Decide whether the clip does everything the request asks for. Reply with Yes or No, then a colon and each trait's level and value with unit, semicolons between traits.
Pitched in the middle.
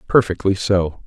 No: low, 100 Hz